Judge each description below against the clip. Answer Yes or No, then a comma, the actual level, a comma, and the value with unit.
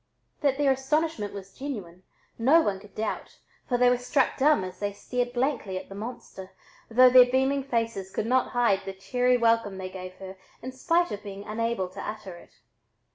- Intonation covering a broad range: No, average, 4.9 semitones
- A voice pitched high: Yes, high, 230 Hz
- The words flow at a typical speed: Yes, average, 190 wpm